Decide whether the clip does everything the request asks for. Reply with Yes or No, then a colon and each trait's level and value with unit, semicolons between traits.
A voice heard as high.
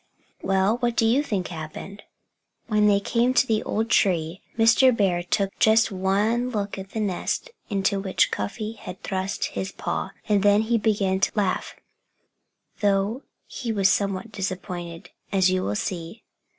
Yes: high, 200 Hz